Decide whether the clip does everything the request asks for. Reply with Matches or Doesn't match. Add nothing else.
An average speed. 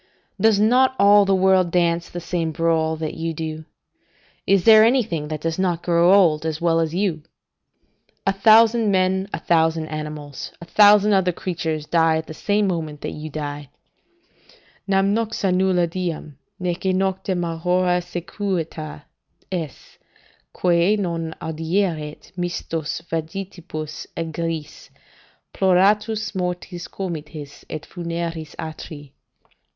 Doesn't match